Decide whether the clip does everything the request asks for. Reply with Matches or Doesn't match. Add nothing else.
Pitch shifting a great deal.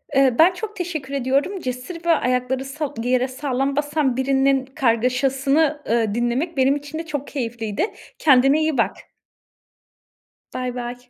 Doesn't match